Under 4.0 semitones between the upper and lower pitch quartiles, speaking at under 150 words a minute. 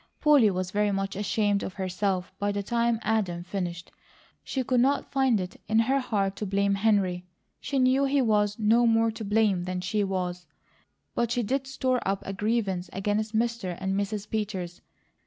No: average, 3.3 semitones; average, 180 wpm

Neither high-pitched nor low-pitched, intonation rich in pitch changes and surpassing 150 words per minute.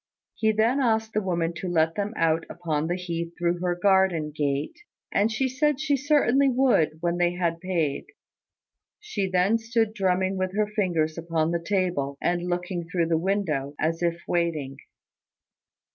No: medium, 180 Hz; average, 4.2 semitones; average, 165 wpm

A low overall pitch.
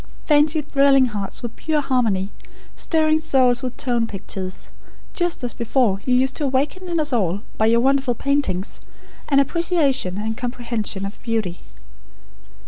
No: very high, 255 Hz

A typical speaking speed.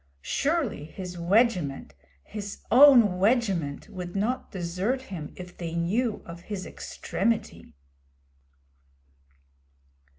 No: slow, 95 wpm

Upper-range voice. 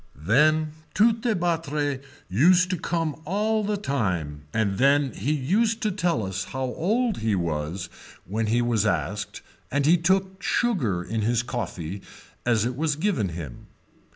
No: medium, 140 Hz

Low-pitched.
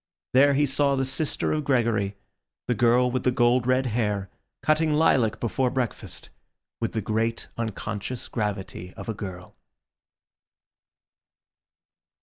Yes: low, 120 Hz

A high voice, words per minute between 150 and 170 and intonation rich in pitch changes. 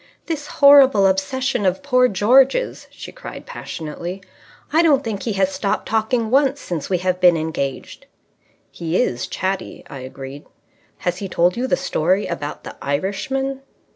Yes: high, 195 Hz; average, 155 wpm; wide, 7.2 semitones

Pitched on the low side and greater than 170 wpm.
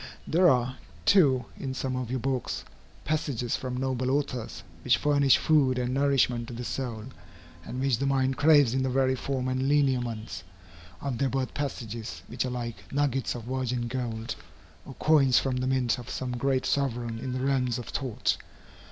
Yes: low, 130 Hz; average, 180 wpm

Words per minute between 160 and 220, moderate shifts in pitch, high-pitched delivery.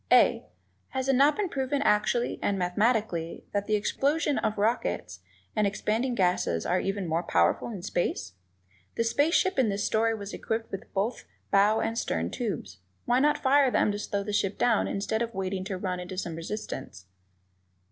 Yes: average, 180 wpm; average, 4.4 semitones; high, 210 Hz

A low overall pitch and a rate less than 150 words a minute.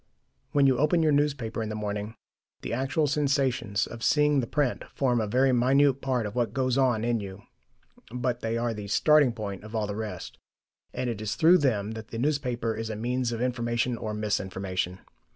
No: low, 120 Hz; fast, 205 wpm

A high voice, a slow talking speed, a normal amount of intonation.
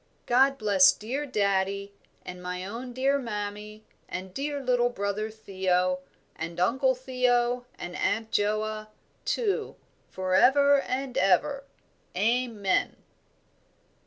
Yes: high, 215 Hz; slow, 110 wpm; average, 4.7 semitones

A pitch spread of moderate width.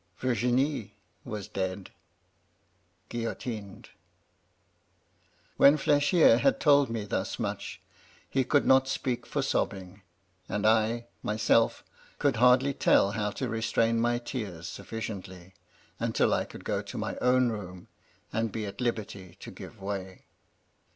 Yes: average, 4.1 semitones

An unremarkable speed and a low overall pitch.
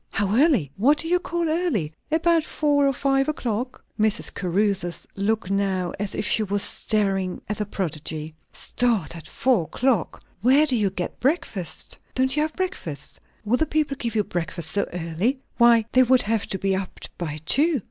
No: average, 180 wpm; high, 215 Hz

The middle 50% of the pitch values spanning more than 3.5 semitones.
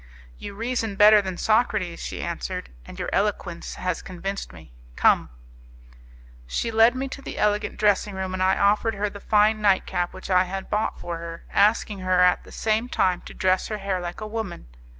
No: average, 2.7 semitones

